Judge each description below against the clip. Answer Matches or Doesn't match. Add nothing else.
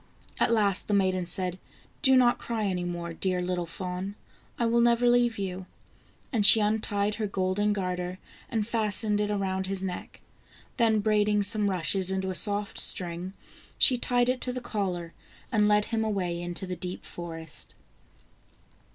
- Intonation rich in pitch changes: Doesn't match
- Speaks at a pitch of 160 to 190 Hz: Doesn't match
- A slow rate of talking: Doesn't match